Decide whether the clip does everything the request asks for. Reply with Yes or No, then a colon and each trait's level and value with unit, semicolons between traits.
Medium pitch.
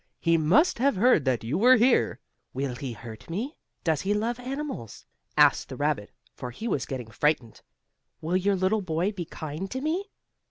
Yes: medium, 180 Hz